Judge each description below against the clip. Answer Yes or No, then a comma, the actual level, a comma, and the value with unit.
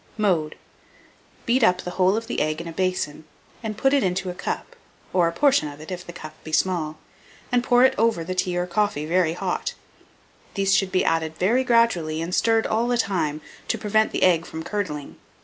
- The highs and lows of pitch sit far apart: No, average, 4.9 semitones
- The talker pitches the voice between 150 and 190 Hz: Yes, medium, 185 Hz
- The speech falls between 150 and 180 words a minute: No, fast, 205 wpm